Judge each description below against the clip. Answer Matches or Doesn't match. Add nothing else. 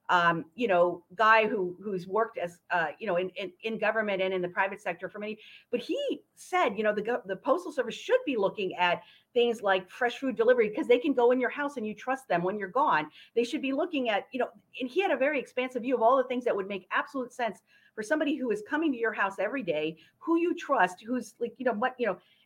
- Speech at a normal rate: Doesn't match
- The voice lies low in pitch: Doesn't match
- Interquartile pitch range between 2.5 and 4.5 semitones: Doesn't match